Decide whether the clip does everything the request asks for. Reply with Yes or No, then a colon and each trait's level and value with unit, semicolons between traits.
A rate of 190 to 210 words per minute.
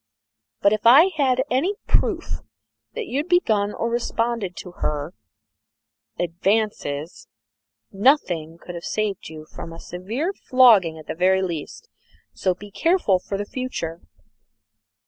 No: average, 145 wpm